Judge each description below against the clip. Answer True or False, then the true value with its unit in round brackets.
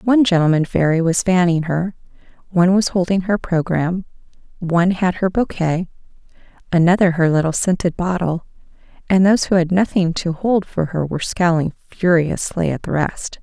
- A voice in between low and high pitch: True (175 Hz)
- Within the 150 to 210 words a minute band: True (155 wpm)